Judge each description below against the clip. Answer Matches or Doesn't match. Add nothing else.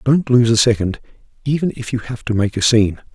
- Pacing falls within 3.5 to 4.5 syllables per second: Doesn't match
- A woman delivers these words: Doesn't match